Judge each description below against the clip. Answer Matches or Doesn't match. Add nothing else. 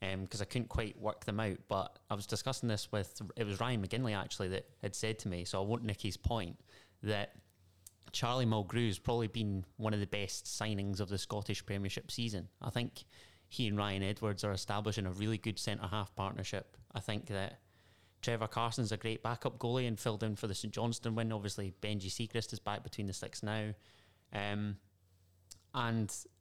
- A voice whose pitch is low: Matches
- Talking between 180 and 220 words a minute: Matches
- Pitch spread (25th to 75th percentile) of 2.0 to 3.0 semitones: Matches